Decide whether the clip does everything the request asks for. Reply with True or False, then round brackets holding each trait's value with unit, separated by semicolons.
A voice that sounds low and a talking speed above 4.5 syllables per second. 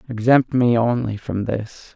False (115 Hz; 4.0 syllables/s)